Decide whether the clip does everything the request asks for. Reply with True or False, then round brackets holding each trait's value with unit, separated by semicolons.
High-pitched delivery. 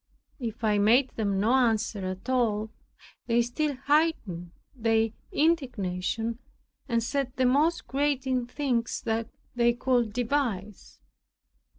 True (240 Hz)